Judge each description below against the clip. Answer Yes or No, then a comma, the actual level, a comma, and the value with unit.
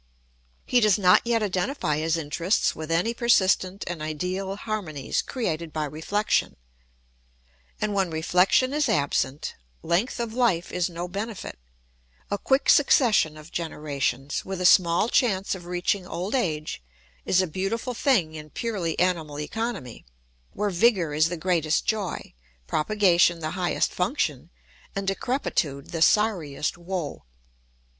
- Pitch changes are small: No, average, 4.8 semitones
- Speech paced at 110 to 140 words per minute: Yes, slow, 135 wpm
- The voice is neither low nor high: Yes, medium, 180 Hz